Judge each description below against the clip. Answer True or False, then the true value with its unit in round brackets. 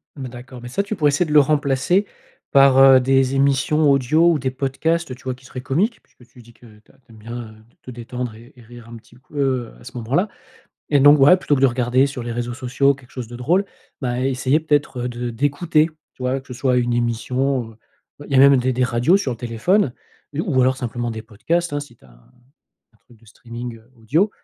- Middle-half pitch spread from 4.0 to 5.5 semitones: False (2.9 semitones)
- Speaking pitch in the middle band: False (130 Hz)